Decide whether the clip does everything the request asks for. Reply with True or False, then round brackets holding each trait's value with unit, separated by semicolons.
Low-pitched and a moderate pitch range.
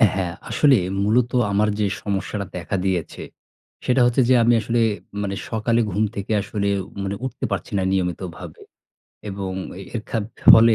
True (105 Hz; 3.3 semitones)